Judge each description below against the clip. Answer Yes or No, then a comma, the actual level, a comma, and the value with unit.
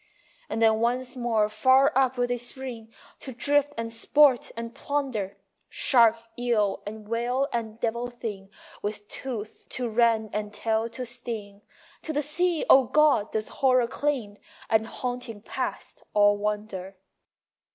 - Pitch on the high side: Yes, high, 235 Hz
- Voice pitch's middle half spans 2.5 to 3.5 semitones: Yes, average, 3.1 semitones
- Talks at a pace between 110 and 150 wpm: Yes, average, 145 wpm